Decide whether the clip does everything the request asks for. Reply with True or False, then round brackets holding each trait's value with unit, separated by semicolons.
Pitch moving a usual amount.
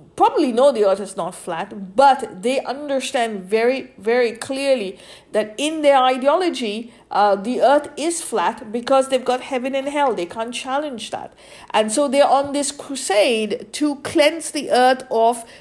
True (4.0 semitones)